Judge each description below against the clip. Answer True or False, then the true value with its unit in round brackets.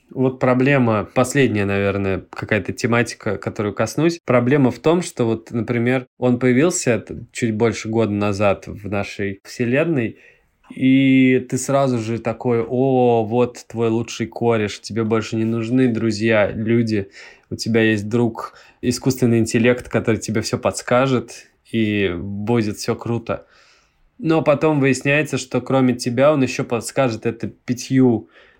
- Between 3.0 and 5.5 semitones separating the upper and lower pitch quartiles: False (2.5 semitones)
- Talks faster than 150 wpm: False (135 wpm)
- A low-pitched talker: True (120 Hz)